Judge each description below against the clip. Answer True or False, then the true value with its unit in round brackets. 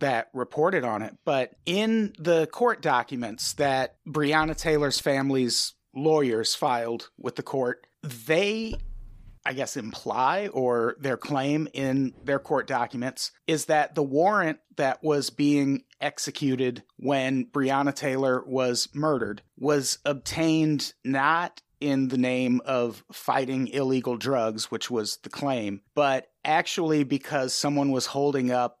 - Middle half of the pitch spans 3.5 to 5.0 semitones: False (2.9 semitones)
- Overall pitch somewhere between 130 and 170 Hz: True (135 Hz)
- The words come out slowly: True (130 wpm)